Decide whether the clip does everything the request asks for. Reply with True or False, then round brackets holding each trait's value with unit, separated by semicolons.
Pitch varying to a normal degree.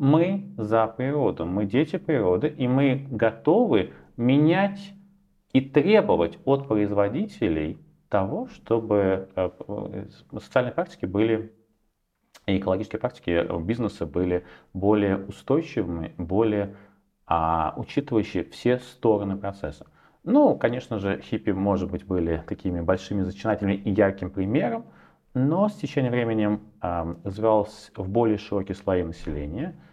True (4.6 semitones)